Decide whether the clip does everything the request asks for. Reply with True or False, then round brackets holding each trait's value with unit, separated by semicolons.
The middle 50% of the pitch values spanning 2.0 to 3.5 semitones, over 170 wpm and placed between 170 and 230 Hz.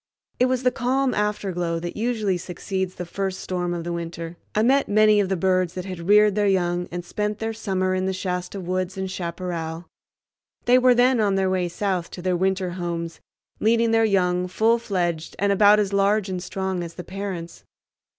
True (2.8 semitones; 200 wpm; 190 Hz)